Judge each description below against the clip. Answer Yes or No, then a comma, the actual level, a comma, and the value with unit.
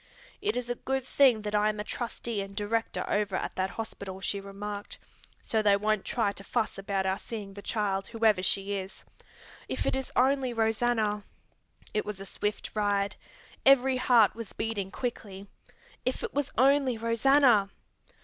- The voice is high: Yes, high, 215 Hz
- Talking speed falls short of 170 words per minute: No, average, 175 wpm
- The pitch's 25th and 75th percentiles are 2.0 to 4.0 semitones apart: Yes, average, 3.3 semitones